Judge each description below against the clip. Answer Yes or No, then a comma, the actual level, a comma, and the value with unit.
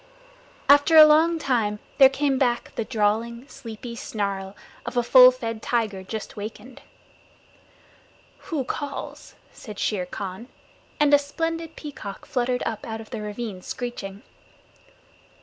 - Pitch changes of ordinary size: Yes, average, 4.6 semitones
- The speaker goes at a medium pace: No, slow, 130 wpm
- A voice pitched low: No, high, 235 Hz